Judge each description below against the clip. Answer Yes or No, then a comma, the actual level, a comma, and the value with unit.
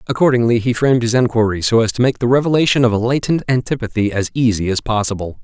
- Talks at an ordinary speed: No, fast, 210 wpm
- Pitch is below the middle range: Yes, low, 120 Hz